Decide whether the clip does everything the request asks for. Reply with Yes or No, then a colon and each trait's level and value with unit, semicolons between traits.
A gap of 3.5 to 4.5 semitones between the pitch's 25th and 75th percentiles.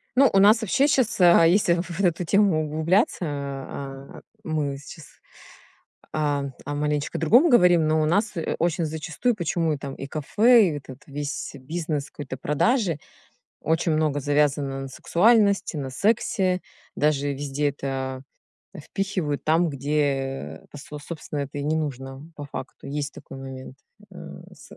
Yes: average, 3.9 semitones